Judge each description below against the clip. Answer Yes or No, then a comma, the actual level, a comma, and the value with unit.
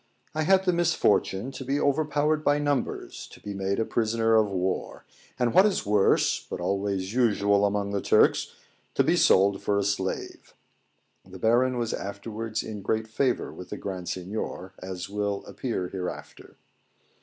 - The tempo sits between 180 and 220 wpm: No, average, 160 wpm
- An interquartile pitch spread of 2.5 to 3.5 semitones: No, average, 4.6 semitones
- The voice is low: Yes, low, 105 Hz